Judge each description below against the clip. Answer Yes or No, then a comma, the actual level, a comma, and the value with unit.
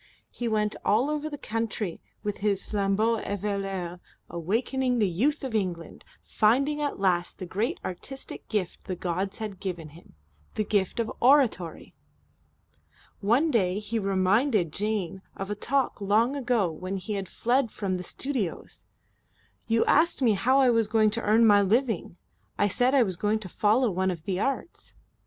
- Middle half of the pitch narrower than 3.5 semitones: No, average, 4.0 semitones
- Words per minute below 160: No, average, 165 wpm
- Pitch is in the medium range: No, high, 210 Hz